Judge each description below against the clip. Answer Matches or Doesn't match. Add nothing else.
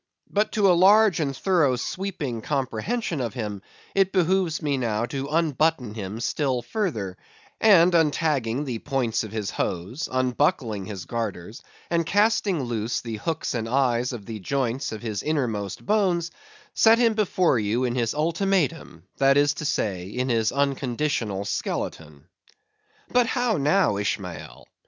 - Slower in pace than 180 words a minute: Matches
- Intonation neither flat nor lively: Doesn't match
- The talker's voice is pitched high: Doesn't match